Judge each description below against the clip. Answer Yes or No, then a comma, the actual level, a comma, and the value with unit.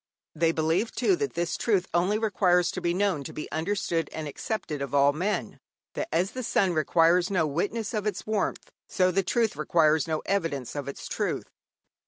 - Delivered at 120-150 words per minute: No, average, 190 wpm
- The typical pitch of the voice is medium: Yes, medium, 175 Hz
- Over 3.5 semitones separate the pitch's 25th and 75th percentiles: Yes, average, 4.5 semitones